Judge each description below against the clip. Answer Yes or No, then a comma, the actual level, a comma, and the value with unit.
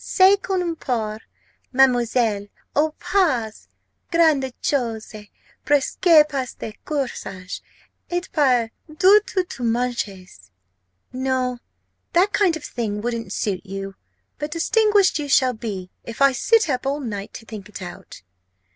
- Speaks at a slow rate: Yes, slow, 130 wpm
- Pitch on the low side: No, very high, 255 Hz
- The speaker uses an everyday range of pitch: No, wide, 6.2 semitones